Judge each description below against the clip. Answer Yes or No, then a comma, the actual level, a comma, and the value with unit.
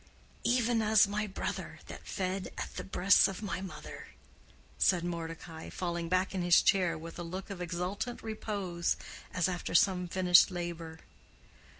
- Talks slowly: No, average, 155 wpm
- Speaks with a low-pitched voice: No, medium, 185 Hz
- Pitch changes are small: Yes, narrow, 2.3 semitones